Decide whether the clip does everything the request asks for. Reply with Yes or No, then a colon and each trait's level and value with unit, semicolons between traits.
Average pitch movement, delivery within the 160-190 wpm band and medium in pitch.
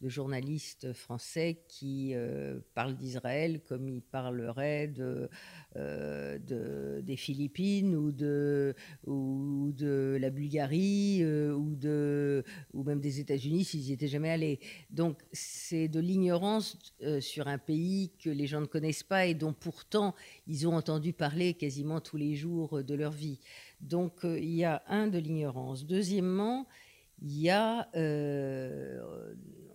No: average, 3.3 semitones; average, 150 wpm; medium, 150 Hz